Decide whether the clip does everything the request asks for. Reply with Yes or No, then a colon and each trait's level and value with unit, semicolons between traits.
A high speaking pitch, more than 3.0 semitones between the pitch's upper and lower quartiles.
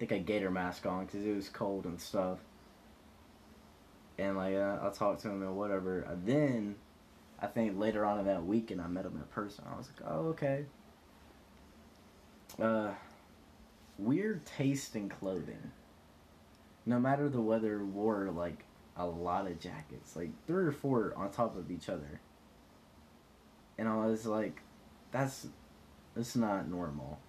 No: low, 100 Hz; average, 4.3 semitones